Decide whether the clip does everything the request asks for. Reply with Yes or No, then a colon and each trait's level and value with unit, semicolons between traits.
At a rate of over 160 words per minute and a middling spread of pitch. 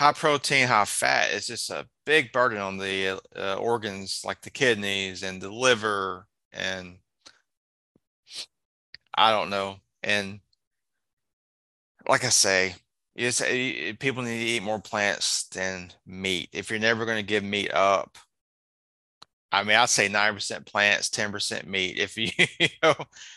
No: average, 150 wpm; average, 3.5 semitones